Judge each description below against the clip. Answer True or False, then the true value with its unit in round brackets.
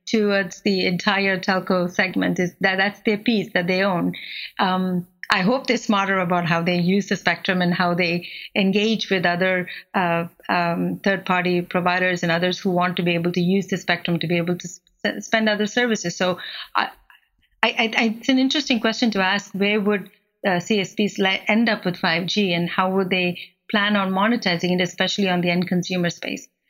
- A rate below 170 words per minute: False (195 wpm)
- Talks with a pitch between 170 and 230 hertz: True (190 Hz)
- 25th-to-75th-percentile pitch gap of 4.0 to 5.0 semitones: False (2.4 semitones)